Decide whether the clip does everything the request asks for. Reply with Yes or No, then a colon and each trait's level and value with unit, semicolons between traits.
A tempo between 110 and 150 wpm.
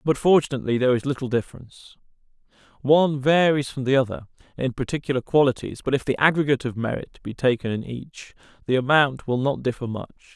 No: average, 175 wpm